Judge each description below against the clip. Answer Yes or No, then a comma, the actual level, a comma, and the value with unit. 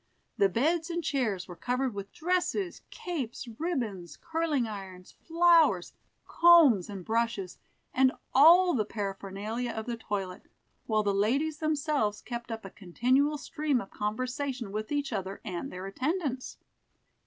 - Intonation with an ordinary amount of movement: No, wide, 7.1 semitones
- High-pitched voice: Yes, high, 240 Hz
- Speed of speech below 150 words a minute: Yes, average, 140 wpm